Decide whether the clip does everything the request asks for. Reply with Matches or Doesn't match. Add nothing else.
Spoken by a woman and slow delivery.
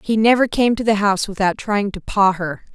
Doesn't match